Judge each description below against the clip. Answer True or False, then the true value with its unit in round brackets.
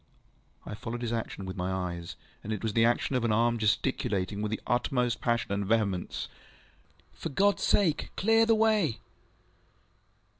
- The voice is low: True (115 Hz)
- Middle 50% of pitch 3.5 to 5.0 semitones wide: True (3.8 semitones)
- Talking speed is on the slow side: False (165 wpm)